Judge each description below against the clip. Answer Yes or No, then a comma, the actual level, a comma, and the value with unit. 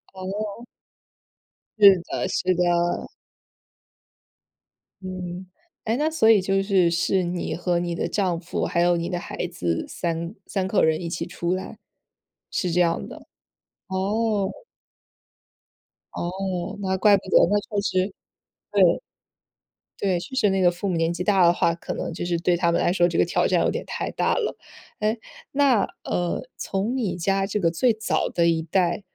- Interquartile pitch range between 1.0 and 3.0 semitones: Yes, narrow, 2.6 semitones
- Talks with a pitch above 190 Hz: No, medium, 185 Hz